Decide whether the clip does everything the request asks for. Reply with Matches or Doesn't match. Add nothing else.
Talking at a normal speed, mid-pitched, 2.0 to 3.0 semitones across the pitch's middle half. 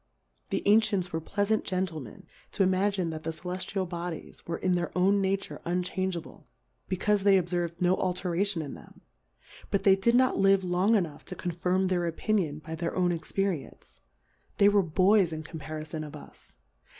Matches